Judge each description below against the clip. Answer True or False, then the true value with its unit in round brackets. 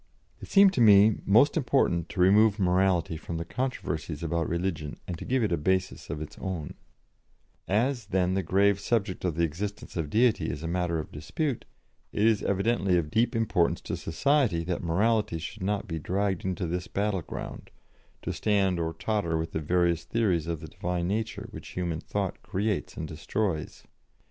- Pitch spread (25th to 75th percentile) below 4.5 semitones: True (4.1 semitones)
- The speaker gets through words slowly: False (180 wpm)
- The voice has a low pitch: True (95 Hz)